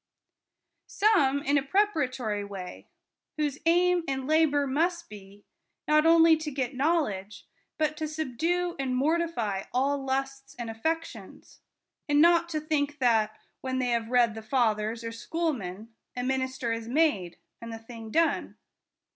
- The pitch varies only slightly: No, wide, 5.5 semitones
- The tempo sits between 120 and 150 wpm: Yes, average, 145 wpm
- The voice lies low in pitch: No, very high, 270 Hz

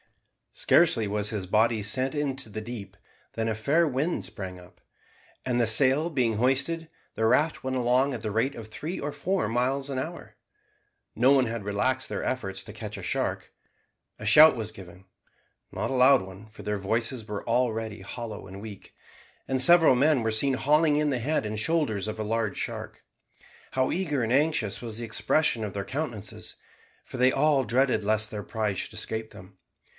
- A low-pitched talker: Yes, low, 120 Hz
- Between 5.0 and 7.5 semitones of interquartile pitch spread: No, average, 4.3 semitones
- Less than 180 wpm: No, average, 190 wpm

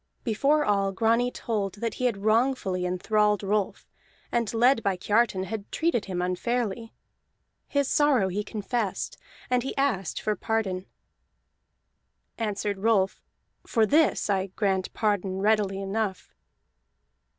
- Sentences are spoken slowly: Yes, slow, 125 wpm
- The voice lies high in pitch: Yes, high, 210 Hz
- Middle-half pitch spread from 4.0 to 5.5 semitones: No, average, 3.3 semitones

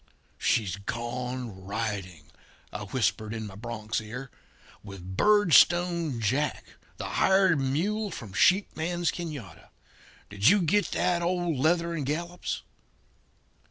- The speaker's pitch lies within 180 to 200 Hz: No, low, 135 Hz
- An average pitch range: No, wide, 8.4 semitones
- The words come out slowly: Yes, slow, 120 wpm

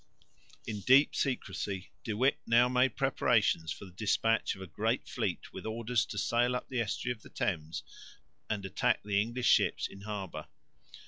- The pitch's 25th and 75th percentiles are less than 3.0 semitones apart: No, average, 3.7 semitones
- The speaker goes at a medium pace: Yes, average, 175 wpm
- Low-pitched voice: Yes, low, 110 Hz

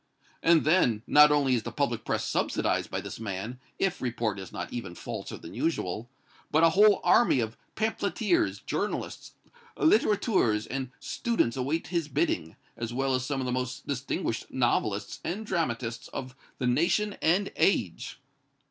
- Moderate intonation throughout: No, wide, 6.6 semitones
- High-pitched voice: No, low, 130 Hz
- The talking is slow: No, average, 155 wpm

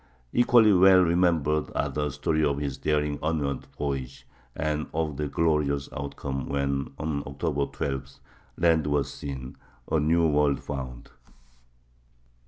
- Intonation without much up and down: Yes, narrow, 2.3 semitones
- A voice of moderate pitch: No, very low, 75 Hz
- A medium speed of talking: No, slow, 125 wpm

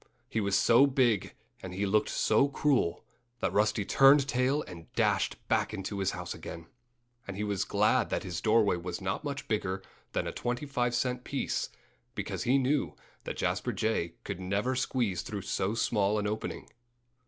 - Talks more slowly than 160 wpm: No, average, 175 wpm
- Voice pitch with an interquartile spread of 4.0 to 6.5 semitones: Yes, average, 4.6 semitones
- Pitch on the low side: Yes, low, 110 Hz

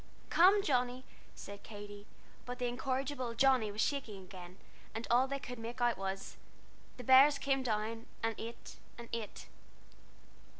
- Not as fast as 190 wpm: Yes, average, 145 wpm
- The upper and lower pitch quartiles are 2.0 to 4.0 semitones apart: Yes, average, 3.5 semitones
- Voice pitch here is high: Yes, high, 240 Hz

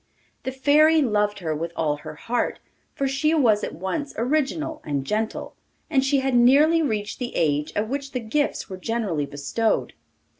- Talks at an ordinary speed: Yes, average, 175 wpm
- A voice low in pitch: No, high, 235 Hz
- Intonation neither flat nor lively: No, wide, 6.8 semitones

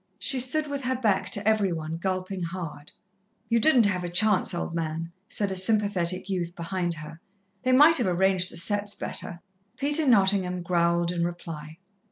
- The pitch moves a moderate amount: Yes, average, 3.7 semitones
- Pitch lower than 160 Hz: No, medium, 185 Hz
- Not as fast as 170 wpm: No, average, 175 wpm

